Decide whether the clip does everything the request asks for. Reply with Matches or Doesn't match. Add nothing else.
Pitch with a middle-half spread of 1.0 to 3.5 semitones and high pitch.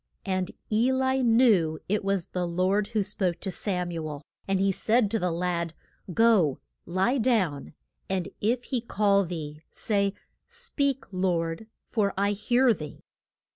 Doesn't match